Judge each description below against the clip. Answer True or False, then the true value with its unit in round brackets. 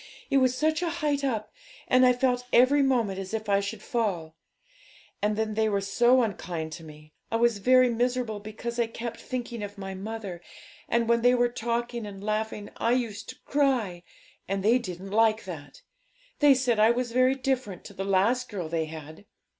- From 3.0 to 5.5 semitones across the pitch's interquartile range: True (4.0 semitones)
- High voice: True (225 Hz)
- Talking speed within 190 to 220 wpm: True (195 wpm)